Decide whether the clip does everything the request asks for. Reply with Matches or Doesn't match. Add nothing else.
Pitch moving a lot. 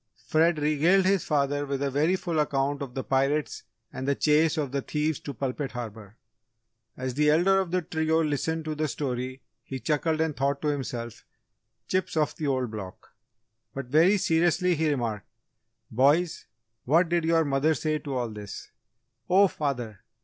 Doesn't match